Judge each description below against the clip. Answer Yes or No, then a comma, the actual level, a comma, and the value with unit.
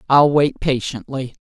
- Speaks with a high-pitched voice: No, medium, 140 Hz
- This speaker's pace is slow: Yes, slow, 125 wpm